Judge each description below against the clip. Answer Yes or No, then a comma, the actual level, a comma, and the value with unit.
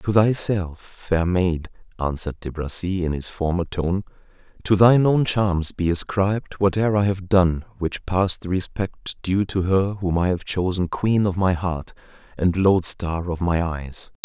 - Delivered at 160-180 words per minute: Yes, average, 170 wpm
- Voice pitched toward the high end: No, very low, 90 Hz